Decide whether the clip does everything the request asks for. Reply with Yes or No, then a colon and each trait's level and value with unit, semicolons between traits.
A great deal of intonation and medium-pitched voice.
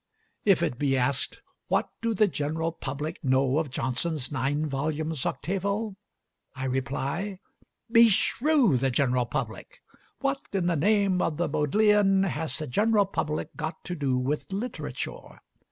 Yes: wide, 6.5 semitones; medium, 160 Hz